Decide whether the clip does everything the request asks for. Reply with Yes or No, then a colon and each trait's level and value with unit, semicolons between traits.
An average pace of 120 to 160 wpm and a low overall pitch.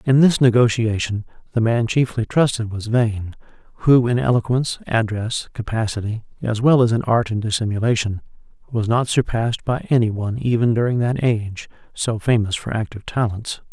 Yes: average, 155 wpm; low, 115 Hz